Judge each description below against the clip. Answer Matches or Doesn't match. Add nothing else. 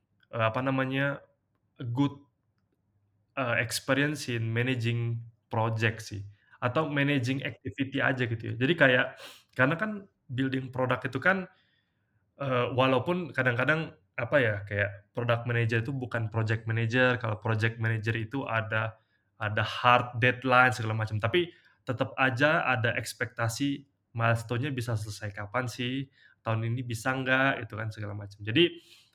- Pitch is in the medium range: Doesn't match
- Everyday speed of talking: Matches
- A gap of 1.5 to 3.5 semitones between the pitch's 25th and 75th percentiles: Matches